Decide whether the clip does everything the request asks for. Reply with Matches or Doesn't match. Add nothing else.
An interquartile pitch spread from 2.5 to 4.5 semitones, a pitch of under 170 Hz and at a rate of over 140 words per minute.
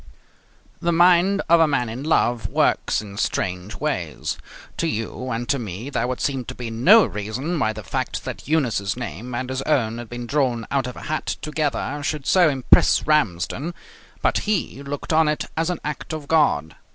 Doesn't match